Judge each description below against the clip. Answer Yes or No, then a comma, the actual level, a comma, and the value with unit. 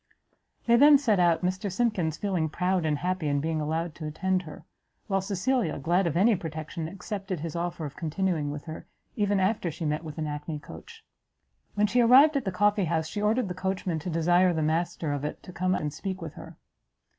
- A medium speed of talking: No, fast, 210 wpm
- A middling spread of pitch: Yes, average, 3.8 semitones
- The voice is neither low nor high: Yes, medium, 175 Hz